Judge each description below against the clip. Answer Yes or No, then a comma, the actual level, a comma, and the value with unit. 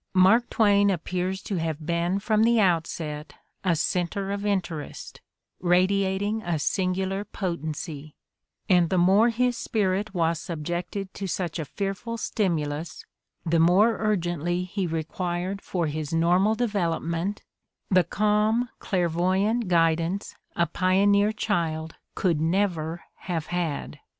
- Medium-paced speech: No, slow, 125 wpm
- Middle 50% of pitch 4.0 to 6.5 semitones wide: No, average, 3.2 semitones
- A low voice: No, medium, 180 Hz